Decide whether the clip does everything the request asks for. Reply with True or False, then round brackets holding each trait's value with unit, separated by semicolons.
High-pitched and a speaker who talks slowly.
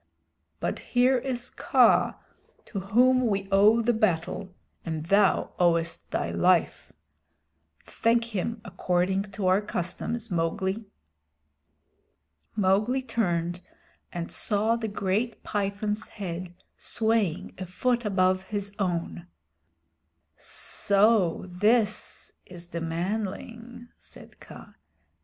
True (200 Hz; 100 wpm)